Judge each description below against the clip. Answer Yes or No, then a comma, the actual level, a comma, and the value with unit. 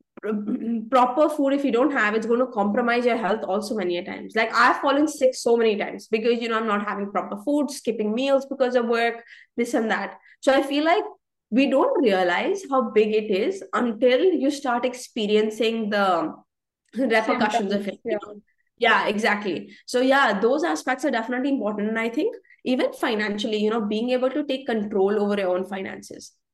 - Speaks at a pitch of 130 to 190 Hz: No, high, 235 Hz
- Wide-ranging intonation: No, average, 3.8 semitones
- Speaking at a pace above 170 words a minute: Yes, average, 190 wpm